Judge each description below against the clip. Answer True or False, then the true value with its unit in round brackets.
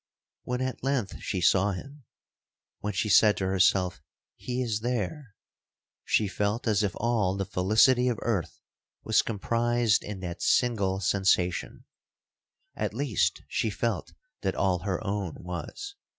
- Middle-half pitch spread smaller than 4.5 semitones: True (3.9 semitones)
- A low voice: True (105 Hz)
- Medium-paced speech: False (130 wpm)